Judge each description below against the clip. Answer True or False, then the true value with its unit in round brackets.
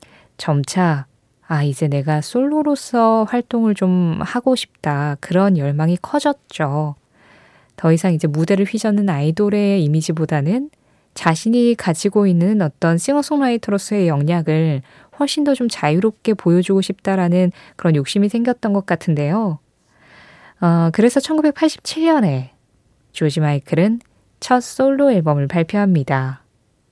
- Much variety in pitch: True (6.7 semitones)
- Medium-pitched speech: True (180 Hz)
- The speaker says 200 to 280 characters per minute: True (270 characters per minute)